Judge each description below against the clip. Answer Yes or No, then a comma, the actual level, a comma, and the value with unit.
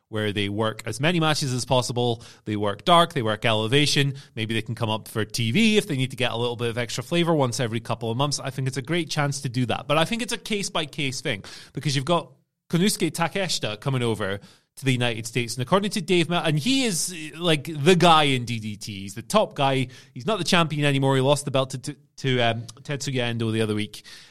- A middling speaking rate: No, fast, 240 wpm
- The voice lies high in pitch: No, low, 135 Hz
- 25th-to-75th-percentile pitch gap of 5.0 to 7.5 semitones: Yes, wide, 5.5 semitones